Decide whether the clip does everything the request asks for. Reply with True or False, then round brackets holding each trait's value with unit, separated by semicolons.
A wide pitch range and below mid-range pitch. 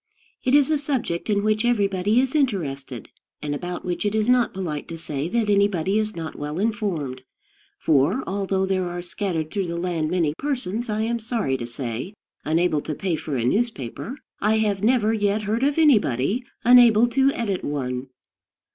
False (6.1 semitones; 195 Hz)